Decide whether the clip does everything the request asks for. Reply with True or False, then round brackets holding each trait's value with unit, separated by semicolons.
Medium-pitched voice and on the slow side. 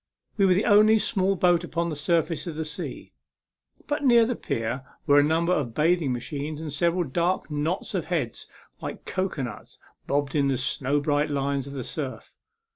False (155 Hz; 185 wpm)